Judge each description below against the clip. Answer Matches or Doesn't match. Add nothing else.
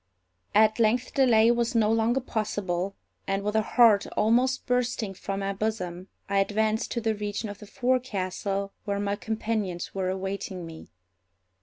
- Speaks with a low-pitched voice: Doesn't match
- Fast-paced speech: Doesn't match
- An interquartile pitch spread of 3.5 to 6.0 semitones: Doesn't match